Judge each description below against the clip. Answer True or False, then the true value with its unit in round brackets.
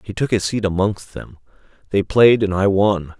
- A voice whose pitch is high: False (100 Hz)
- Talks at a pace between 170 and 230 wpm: True (205 wpm)